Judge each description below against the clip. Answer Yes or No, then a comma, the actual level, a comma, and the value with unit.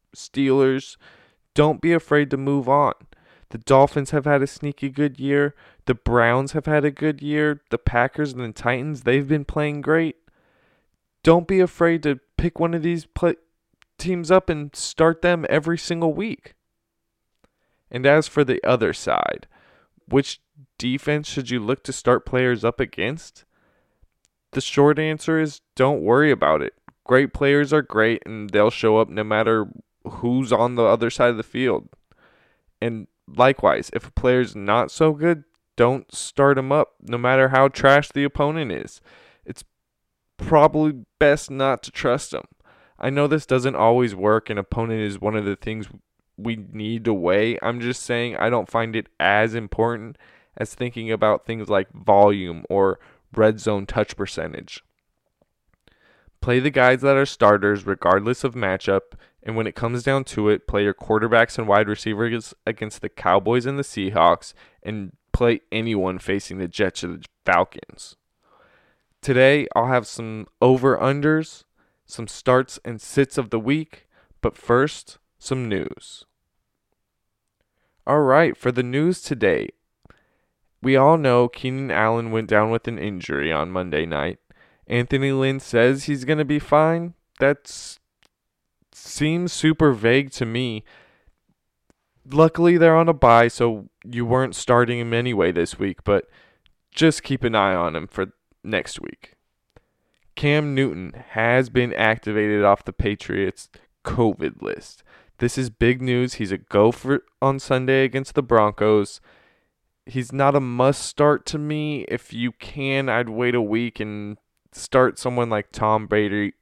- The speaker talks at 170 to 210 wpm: No, average, 155 wpm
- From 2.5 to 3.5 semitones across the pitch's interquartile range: No, average, 4.5 semitones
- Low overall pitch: Yes, low, 125 Hz